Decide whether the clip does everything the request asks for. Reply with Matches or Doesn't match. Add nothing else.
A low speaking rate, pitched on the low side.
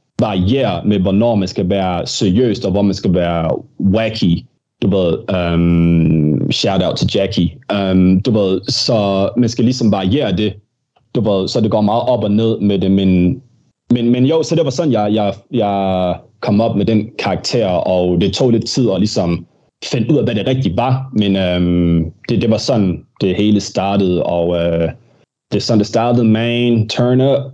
Doesn't match